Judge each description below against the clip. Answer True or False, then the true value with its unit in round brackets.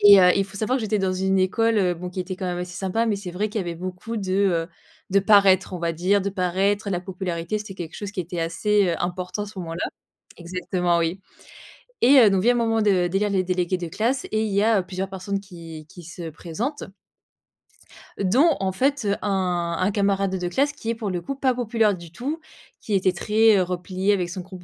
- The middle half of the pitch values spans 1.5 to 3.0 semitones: True (2.7 semitones)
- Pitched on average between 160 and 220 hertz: True (190 Hz)